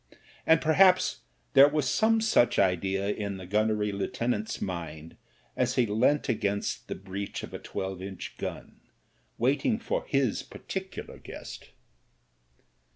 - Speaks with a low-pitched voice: Yes, low, 110 Hz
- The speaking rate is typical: No, slow, 130 wpm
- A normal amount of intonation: No, wide, 6.3 semitones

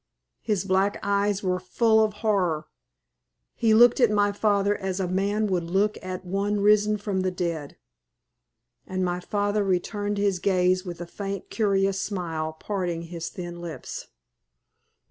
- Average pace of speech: Yes, average, 150 wpm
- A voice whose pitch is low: No, high, 195 Hz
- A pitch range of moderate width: No, narrow, 2.3 semitones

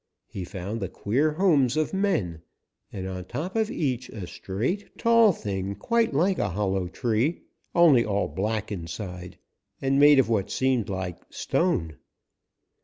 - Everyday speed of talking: Yes, average, 150 wpm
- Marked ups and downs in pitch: Yes, wide, 8.5 semitones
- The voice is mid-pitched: No, low, 115 Hz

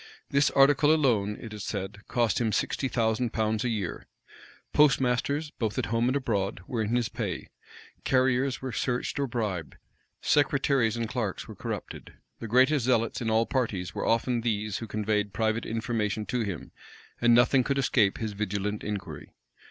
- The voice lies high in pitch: No, low, 115 Hz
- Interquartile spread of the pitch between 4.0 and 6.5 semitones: No, average, 3.2 semitones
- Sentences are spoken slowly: No, average, 165 wpm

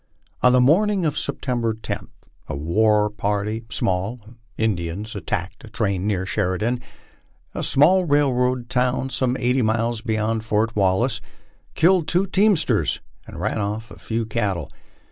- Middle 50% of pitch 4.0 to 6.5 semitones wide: No, average, 3.5 semitones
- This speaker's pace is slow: No, average, 145 wpm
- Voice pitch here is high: No, low, 115 Hz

